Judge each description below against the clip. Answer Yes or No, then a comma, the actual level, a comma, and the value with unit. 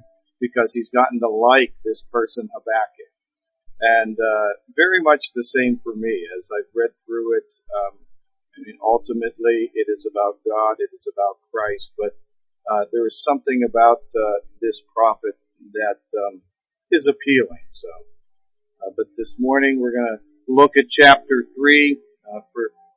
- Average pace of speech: Yes, average, 155 wpm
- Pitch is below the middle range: No, medium, 145 Hz